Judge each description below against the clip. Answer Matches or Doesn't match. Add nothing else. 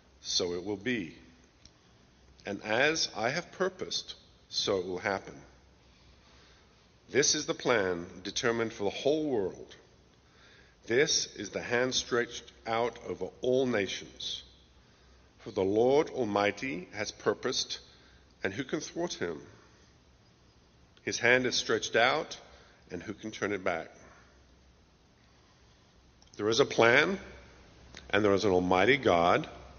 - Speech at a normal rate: Doesn't match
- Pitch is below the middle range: Matches